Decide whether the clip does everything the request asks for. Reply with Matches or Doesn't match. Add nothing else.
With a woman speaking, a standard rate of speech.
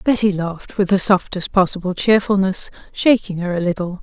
Matches